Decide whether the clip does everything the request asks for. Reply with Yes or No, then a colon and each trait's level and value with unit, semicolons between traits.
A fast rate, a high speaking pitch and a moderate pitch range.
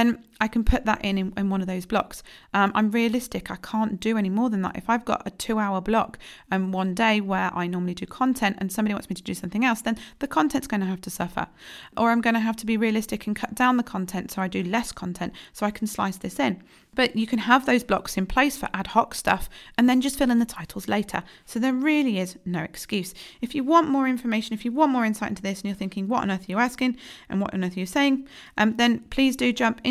Yes: fast, 275 wpm; high, 220 Hz; average, 4.1 semitones